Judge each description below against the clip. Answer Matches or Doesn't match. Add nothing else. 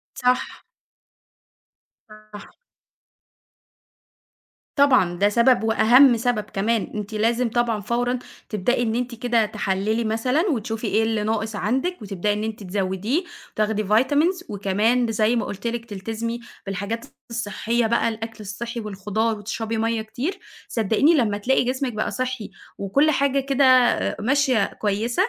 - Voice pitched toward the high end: Matches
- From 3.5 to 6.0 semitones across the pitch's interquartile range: Doesn't match